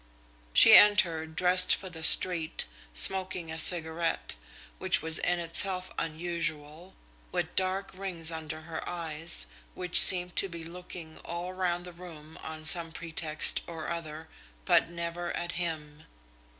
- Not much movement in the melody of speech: Yes, narrow, 1.9 semitones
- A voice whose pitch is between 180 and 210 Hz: No, medium, 170 Hz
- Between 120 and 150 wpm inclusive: Yes, slow, 135 wpm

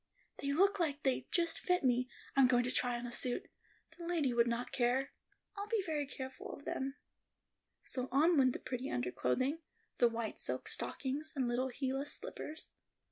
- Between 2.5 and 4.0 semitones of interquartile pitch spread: Yes, average, 3.6 semitones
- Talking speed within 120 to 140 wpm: No, average, 165 wpm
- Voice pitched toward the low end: No, very high, 265 Hz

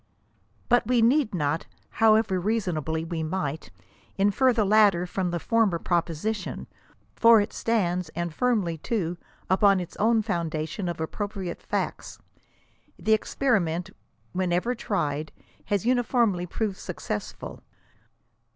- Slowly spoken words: Yes, slow, 125 wpm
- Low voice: No, high, 190 Hz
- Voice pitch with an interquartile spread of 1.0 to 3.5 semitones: No, average, 4.5 semitones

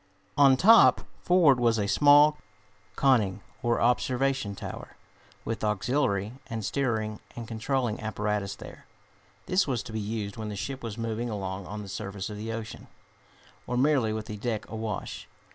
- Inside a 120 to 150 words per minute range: No, average, 160 wpm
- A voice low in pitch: Yes, low, 115 Hz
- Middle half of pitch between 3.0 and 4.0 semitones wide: Yes, average, 3.7 semitones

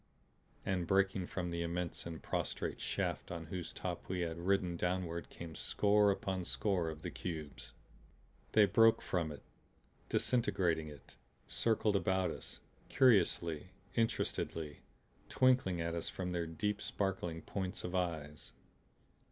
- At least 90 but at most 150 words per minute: Yes, slow, 135 wpm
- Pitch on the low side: Yes, very low, 90 Hz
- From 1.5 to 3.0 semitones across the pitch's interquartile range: Yes, average, 2.7 semitones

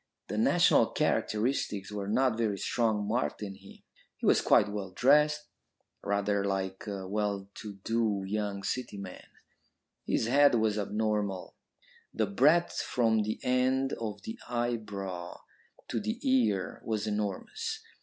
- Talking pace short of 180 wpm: Yes, slow, 135 wpm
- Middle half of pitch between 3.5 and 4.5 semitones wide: Yes, average, 3.9 semitones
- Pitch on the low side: Yes, low, 105 Hz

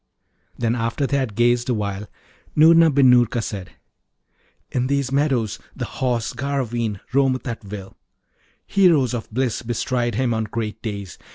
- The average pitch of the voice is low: Yes, low, 120 Hz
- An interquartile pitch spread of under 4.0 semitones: Yes, average, 3.3 semitones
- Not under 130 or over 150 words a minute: Yes, average, 145 wpm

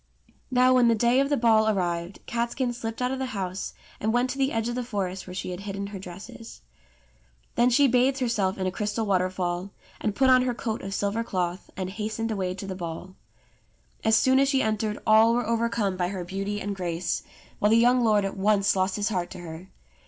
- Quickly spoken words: Yes, fast, 220 wpm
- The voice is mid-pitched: No, high, 210 Hz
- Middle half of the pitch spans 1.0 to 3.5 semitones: No, average, 4.0 semitones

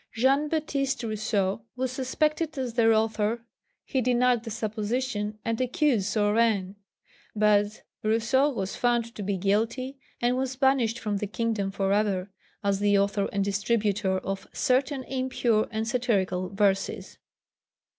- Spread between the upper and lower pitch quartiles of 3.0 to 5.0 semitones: Yes, average, 3.8 semitones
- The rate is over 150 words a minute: No, slow, 135 wpm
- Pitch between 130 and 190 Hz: No, high, 225 Hz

